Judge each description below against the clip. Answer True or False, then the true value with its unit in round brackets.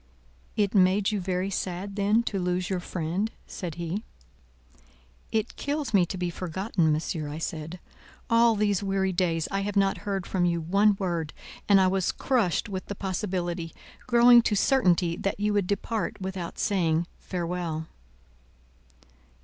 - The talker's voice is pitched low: False (190 Hz)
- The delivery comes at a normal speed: True (155 wpm)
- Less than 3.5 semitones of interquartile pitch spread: True (2.8 semitones)